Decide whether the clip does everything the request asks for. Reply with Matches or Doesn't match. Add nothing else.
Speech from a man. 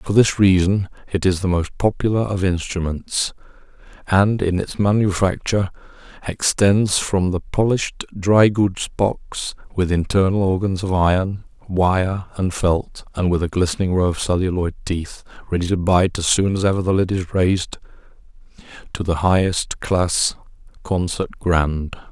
Matches